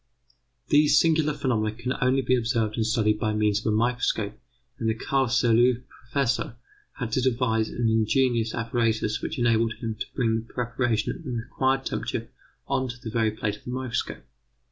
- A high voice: No, low, 115 Hz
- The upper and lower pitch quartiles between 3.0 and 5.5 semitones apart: No, narrow, 2.4 semitones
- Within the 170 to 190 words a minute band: Yes, average, 175 wpm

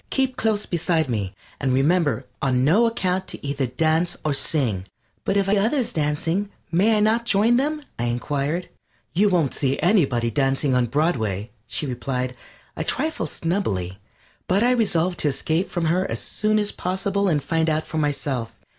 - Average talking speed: Yes, average, 175 wpm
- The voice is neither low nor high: Yes, medium, 160 Hz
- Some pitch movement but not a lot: No, wide, 6.9 semitones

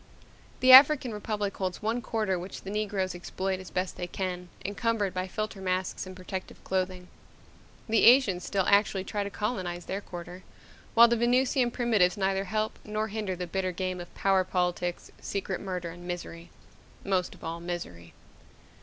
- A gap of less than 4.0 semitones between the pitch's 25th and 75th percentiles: Yes, average, 2.9 semitones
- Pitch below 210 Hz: Yes, high, 190 Hz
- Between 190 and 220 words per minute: No, average, 165 wpm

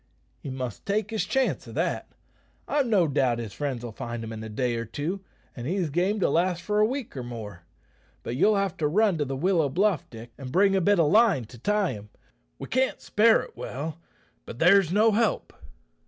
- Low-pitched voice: No, medium, 165 Hz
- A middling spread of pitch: No, wide, 8.7 semitones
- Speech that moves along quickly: Yes, fast, 215 wpm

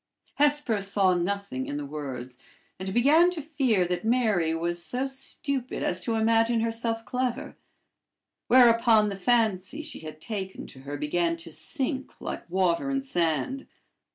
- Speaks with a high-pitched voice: Yes, high, 215 Hz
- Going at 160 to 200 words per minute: No, average, 150 wpm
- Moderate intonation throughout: No, wide, 6.7 semitones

